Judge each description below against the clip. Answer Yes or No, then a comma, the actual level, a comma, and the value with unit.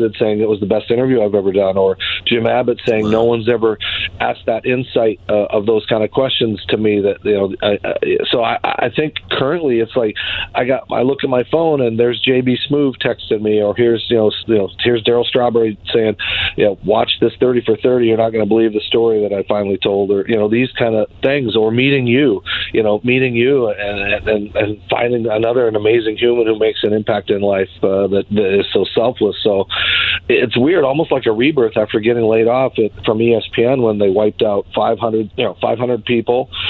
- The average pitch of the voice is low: Yes, low, 115 Hz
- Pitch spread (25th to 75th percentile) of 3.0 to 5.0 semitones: No, narrow, 2.6 semitones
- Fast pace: Yes, fast, 225 wpm